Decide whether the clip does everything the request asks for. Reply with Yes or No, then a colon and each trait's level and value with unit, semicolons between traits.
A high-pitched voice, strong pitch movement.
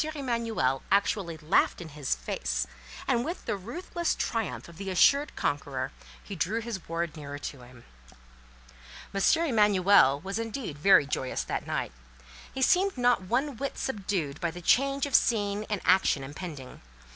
Yes: high, 195 Hz; wide, 8.0 semitones